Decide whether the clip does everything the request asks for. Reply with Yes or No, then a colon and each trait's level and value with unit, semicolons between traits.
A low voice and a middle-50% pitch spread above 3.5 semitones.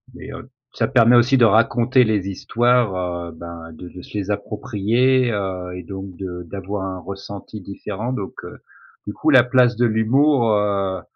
Yes: low, 105 Hz; average, 4.2 semitones